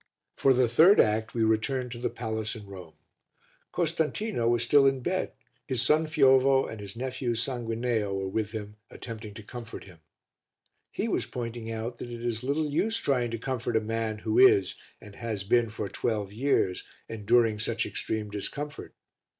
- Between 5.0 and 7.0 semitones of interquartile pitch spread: No, average, 3.3 semitones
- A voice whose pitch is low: Yes, low, 115 Hz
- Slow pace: No, average, 175 wpm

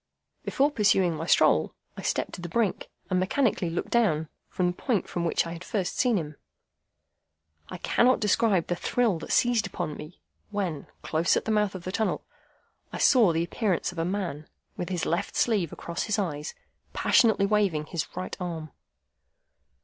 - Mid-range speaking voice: Yes, medium, 180 Hz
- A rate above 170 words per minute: Yes, average, 180 wpm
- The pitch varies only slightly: No, average, 4.2 semitones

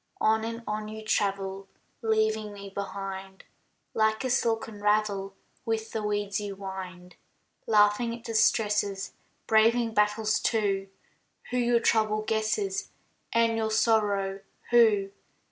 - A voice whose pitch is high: Yes, high, 215 Hz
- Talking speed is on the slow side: Yes, slow, 120 wpm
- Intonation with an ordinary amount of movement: No, narrow, 2.0 semitones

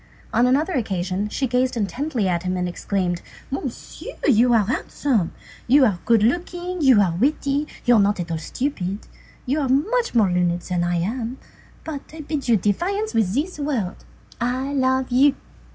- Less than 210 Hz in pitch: No, high, 245 Hz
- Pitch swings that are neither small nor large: No, wide, 6.5 semitones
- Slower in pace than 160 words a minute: No, average, 175 wpm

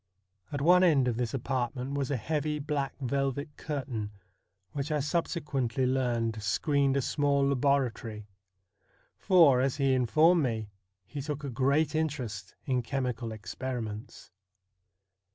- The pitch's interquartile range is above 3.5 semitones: No, average, 3.0 semitones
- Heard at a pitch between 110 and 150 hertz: Yes, low, 135 Hz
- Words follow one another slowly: Yes, slow, 130 wpm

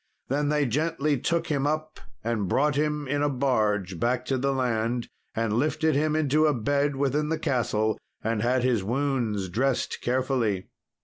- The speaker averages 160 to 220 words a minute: Yes, average, 170 wpm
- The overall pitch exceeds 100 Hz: Yes, low, 135 Hz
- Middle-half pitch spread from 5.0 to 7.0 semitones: No, average, 4.2 semitones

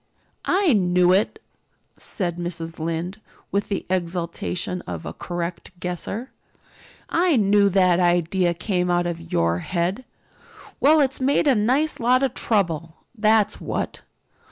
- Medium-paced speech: No, slow, 130 wpm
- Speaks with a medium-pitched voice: Yes, medium, 180 Hz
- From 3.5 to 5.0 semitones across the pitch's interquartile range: Yes, average, 3.9 semitones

